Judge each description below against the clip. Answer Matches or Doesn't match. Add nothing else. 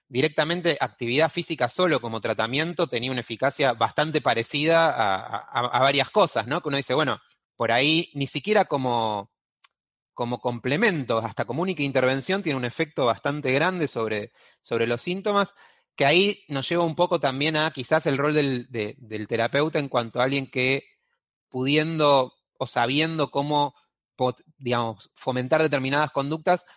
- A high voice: Doesn't match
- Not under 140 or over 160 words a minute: Matches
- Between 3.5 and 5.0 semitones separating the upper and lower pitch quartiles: Matches